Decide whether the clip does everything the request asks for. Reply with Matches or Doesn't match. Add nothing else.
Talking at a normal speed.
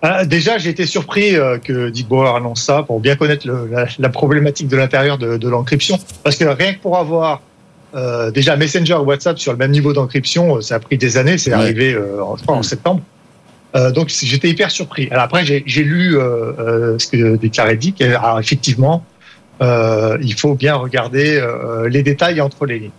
Matches